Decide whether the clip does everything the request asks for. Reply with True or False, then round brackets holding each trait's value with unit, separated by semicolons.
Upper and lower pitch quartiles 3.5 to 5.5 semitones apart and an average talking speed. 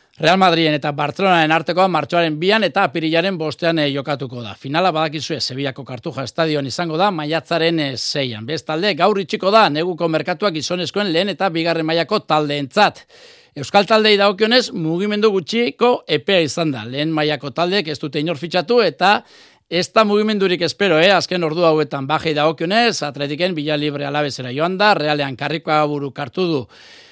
True (4.4 semitones; 160 wpm)